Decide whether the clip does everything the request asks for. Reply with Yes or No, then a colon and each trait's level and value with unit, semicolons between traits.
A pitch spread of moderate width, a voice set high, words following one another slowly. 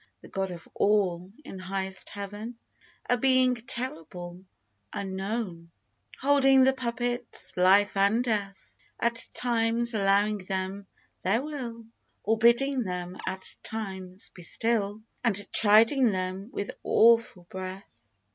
Yes: average, 3.9 semitones; high, 205 Hz; slow, 125 wpm